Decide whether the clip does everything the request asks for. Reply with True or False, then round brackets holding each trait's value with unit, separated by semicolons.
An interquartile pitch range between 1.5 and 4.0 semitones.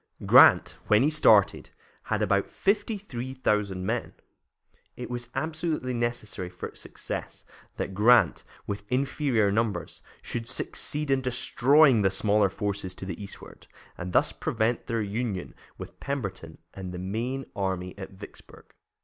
False (4.7 semitones)